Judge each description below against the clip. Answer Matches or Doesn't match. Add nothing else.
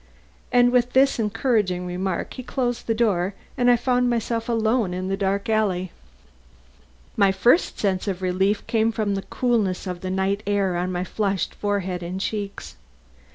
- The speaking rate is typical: Matches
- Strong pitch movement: Doesn't match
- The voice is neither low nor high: Doesn't match